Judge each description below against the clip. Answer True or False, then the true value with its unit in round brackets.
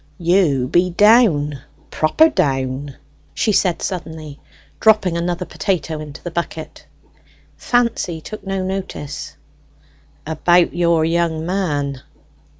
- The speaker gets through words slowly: True (105 wpm)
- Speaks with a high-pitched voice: False (170 Hz)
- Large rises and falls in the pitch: False (3.8 semitones)